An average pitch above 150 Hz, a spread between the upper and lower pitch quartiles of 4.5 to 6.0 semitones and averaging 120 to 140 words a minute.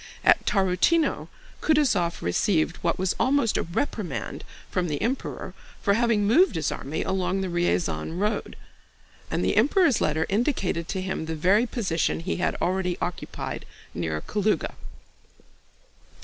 Yes: high, 190 Hz; average, 4.8 semitones; slow, 135 wpm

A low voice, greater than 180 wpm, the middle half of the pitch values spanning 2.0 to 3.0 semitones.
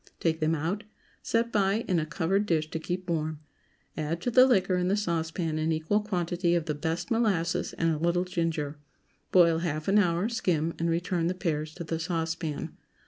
No: medium, 170 Hz; average, 195 wpm; narrow, 2.5 semitones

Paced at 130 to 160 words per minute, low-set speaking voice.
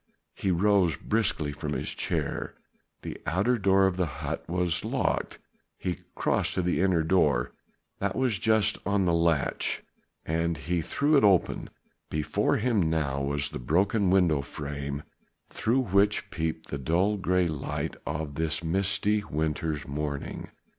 Yes: average, 145 wpm; very low, 85 Hz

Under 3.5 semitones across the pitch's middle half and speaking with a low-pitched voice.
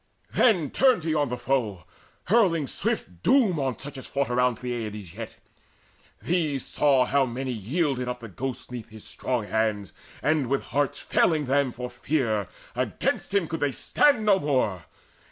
No: average, 4.8 semitones; low, 130 Hz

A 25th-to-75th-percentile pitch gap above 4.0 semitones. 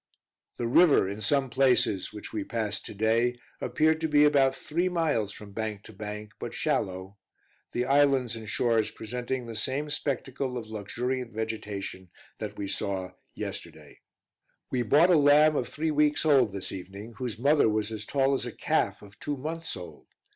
Yes: average, 5.2 semitones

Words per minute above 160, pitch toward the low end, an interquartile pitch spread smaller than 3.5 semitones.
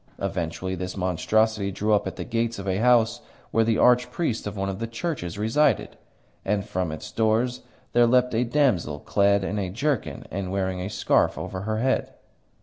No: average, 185 wpm; low, 105 Hz; average, 3.8 semitones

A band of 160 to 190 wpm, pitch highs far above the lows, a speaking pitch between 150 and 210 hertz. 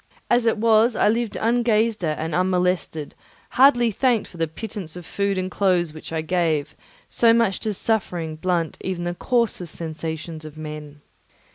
Yes: average, 165 wpm; wide, 5.7 semitones; medium, 185 Hz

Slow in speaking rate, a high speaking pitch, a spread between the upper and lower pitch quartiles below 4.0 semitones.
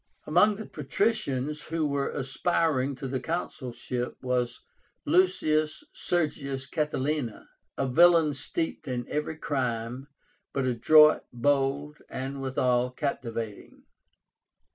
No: slow, 100 wpm; medium, 140 Hz; average, 3.4 semitones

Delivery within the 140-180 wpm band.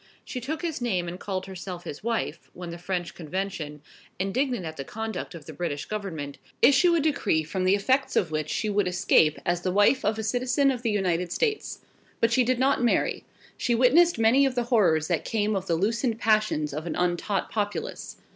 No: fast, 205 wpm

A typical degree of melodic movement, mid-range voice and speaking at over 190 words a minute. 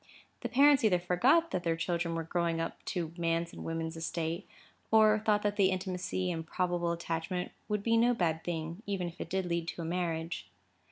Yes: average, 3.1 semitones; medium, 175 Hz; average, 200 wpm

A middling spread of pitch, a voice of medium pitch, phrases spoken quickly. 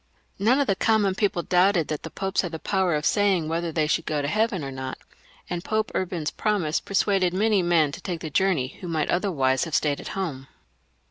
Yes: average, 4.1 semitones; medium, 175 Hz; fast, 215 wpm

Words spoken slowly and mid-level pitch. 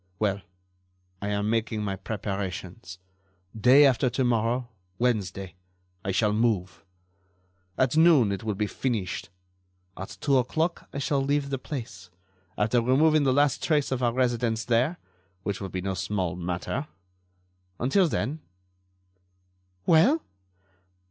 No: slow, 130 wpm; low, 115 Hz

